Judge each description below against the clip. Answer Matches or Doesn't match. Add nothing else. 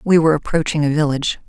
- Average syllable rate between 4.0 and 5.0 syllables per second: Doesn't match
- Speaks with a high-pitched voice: Doesn't match